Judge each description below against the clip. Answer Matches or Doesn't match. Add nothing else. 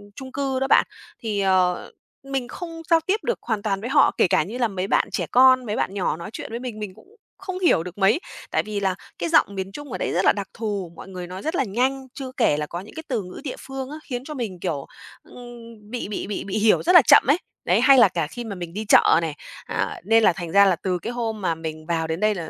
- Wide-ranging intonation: Matches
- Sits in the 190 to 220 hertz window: Matches